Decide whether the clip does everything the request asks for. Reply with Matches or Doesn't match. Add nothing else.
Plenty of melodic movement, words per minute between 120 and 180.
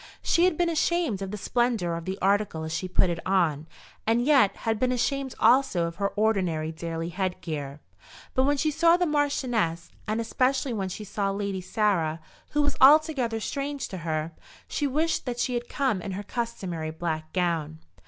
Doesn't match